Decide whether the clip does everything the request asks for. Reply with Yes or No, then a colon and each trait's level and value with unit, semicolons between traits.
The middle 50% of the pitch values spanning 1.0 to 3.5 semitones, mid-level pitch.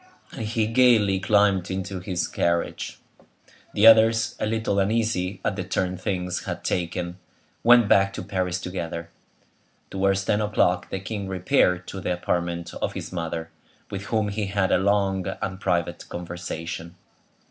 No: narrow, 2.6 semitones; very low, 95 Hz